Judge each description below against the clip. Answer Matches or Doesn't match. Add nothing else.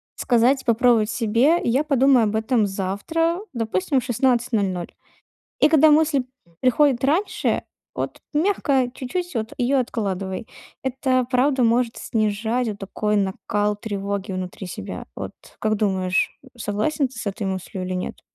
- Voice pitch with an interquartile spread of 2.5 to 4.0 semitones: Doesn't match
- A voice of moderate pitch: Doesn't match